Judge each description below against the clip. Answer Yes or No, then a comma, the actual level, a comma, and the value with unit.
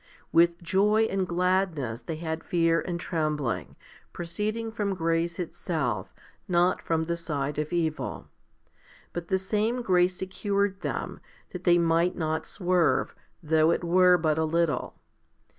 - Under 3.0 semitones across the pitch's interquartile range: Yes, narrow, 2.5 semitones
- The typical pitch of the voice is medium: Yes, medium, 170 Hz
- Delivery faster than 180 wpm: No, average, 140 wpm